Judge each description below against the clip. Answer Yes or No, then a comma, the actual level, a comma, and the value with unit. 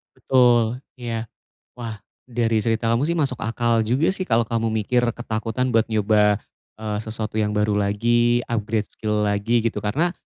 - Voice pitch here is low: Yes, low, 115 Hz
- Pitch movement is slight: Yes, narrow, 2.0 semitones